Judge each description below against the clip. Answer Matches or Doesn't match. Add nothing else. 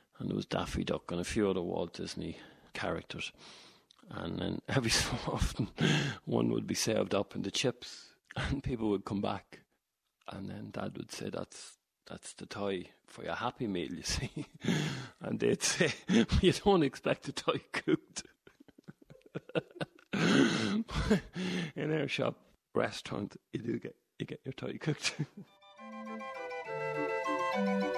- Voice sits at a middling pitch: Matches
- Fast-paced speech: Doesn't match